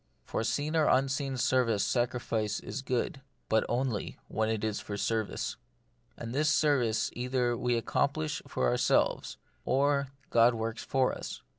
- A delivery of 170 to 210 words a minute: No, average, 150 wpm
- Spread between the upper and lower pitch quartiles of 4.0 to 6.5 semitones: No, average, 3.2 semitones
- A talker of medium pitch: No, low, 120 Hz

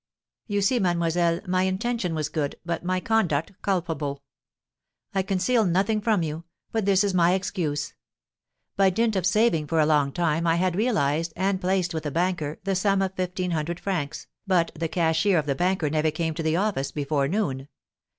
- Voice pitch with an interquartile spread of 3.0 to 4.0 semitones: Yes, average, 3.5 semitones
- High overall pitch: No, medium, 175 Hz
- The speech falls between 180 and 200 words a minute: Yes, average, 185 wpm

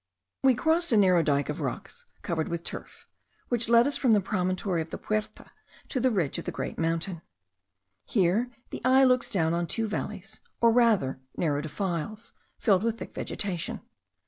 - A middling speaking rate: Yes, average, 175 wpm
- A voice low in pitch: No, high, 200 Hz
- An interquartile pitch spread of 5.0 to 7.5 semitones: Yes, wide, 5.5 semitones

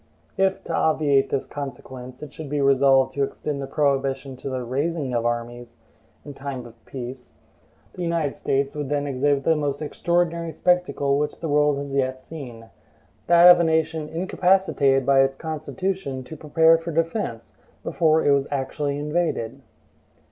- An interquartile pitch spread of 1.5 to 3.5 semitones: Yes, average, 3.2 semitones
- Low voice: No, medium, 145 Hz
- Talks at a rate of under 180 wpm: Yes, average, 160 wpm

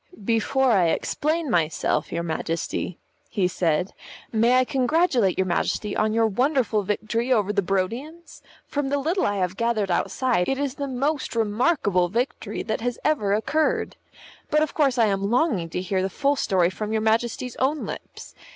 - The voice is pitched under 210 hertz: No, high, 225 Hz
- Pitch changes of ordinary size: No, wide, 5.7 semitones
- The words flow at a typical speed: Yes, average, 170 wpm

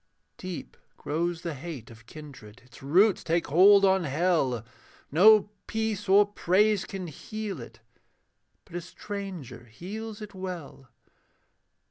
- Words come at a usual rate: No, slow, 125 wpm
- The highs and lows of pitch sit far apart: Yes, wide, 6.3 semitones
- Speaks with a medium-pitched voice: Yes, medium, 175 Hz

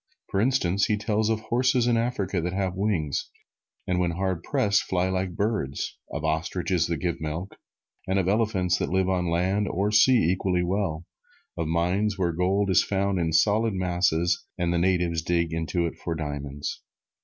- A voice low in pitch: Yes, very low, 90 Hz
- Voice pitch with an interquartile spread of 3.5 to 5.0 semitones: No, average, 2.9 semitones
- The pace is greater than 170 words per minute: Yes, average, 180 wpm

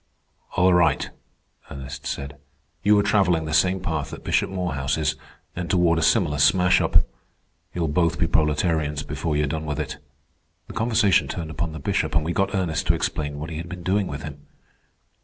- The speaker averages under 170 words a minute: No, average, 190 wpm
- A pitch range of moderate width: Yes, average, 3.3 semitones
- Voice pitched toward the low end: Yes, very low, 80 Hz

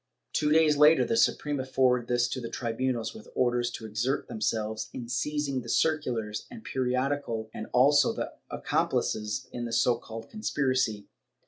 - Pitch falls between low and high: No, low, 125 Hz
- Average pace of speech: Yes, average, 160 wpm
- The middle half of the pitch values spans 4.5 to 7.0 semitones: No, average, 3.9 semitones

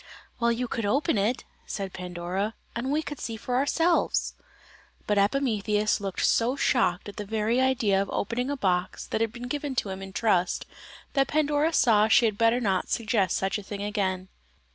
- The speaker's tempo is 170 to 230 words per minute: Yes, average, 185 wpm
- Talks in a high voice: Yes, high, 220 Hz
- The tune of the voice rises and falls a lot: No, average, 4.1 semitones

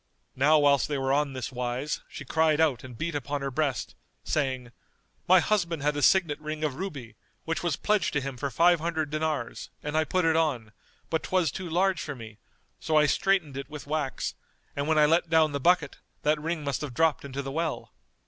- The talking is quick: Yes, fast, 215 wpm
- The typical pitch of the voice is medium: Yes, medium, 150 Hz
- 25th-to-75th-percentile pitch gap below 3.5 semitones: Yes, average, 2.9 semitones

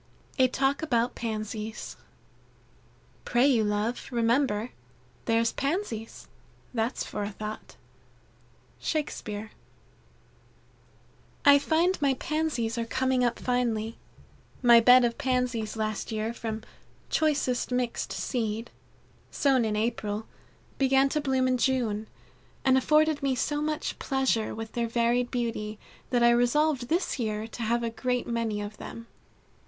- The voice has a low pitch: No, high, 240 Hz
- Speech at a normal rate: No, slow, 125 wpm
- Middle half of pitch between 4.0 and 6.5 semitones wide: No, average, 3.0 semitones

